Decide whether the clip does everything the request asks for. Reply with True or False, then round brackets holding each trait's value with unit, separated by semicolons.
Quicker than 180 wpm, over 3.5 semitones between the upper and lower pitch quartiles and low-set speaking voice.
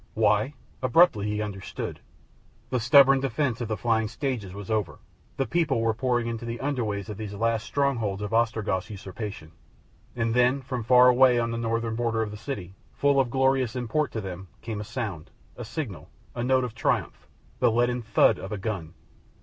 False (190 wpm; 3.1 semitones; 115 Hz)